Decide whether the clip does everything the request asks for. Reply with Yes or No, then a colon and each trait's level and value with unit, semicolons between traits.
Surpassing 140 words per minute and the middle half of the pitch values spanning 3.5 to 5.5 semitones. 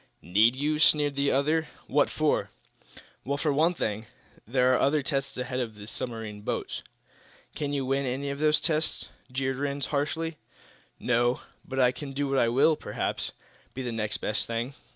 No: average, 175 wpm; average, 2.8 semitones